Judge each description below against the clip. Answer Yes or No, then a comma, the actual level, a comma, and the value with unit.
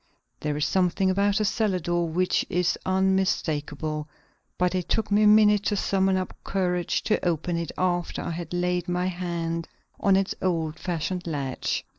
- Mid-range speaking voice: Yes, medium, 180 Hz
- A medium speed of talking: Yes, average, 170 wpm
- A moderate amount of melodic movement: No, narrow, 2.3 semitones